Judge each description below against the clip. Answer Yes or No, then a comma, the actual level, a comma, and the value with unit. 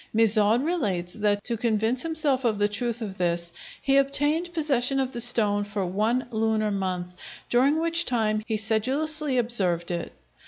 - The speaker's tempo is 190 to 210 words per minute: No, average, 160 wpm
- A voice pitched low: No, high, 225 Hz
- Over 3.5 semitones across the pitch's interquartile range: Yes, average, 4.7 semitones